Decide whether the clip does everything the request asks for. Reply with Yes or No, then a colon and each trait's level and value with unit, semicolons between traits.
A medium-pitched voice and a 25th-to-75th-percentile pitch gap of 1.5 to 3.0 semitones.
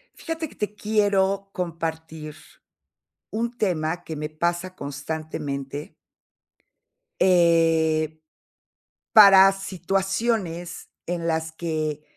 No: medium, 170 Hz; average, 3.6 semitones